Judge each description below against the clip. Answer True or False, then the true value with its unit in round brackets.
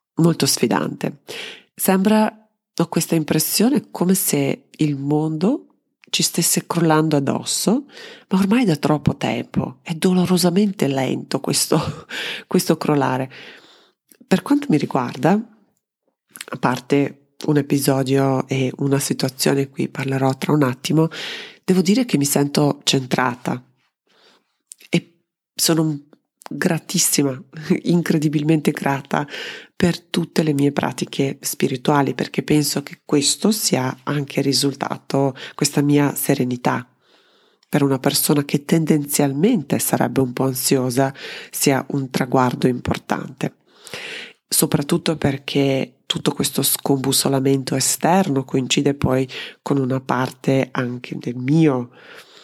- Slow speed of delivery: True (110 wpm)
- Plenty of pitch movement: False (4.6 semitones)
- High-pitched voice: False (150 Hz)